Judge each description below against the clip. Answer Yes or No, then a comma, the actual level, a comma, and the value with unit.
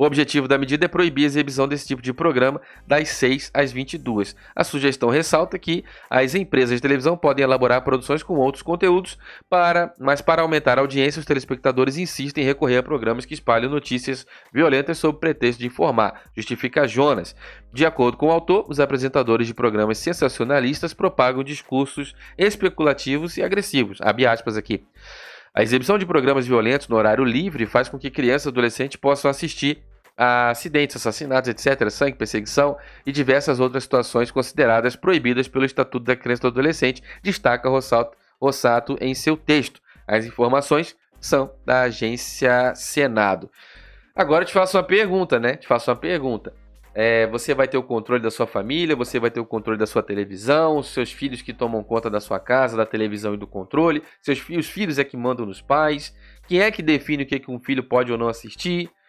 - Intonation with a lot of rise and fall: No, average, 3.6 semitones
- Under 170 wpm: No, fast, 185 wpm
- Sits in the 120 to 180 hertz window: Yes, low, 135 Hz